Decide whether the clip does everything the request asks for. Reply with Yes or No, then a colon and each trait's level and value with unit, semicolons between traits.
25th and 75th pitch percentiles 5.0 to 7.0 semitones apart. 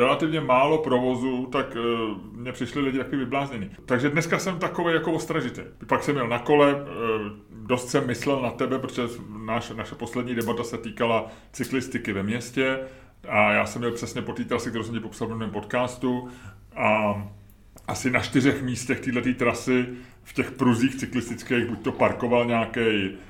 No: narrow, 2.6 semitones